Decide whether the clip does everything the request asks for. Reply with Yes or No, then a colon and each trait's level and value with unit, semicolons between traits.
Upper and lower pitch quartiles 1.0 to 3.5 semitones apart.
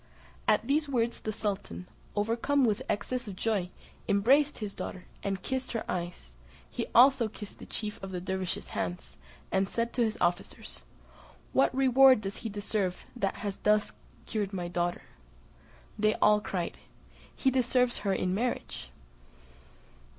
No: average, 4.2 semitones